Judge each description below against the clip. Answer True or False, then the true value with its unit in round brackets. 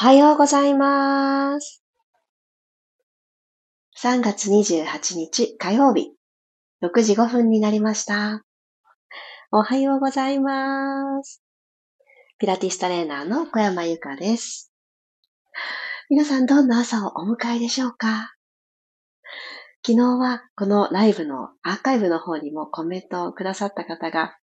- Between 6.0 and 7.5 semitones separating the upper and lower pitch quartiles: False (5.6 semitones)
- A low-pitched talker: False (235 Hz)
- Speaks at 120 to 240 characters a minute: True (230 characters per minute)